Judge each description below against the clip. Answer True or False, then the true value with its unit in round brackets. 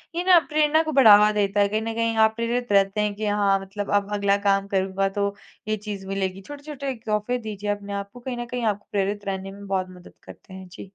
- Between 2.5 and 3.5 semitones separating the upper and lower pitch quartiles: True (2.8 semitones)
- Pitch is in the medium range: False (205 Hz)